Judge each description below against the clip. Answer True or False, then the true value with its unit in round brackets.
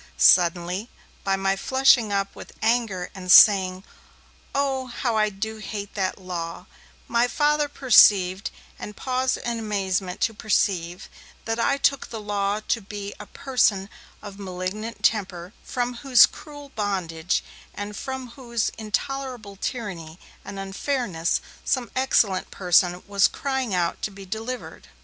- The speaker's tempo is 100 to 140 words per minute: True (135 wpm)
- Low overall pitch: False (210 Hz)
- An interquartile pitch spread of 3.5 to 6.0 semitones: True (4.4 semitones)